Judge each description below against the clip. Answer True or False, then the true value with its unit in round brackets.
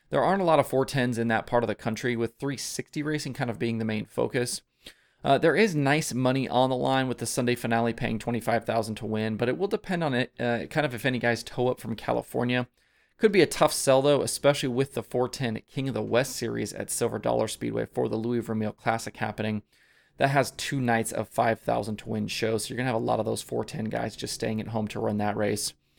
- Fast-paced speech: True (245 wpm)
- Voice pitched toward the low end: True (120 Hz)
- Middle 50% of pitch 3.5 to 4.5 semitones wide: False (3.0 semitones)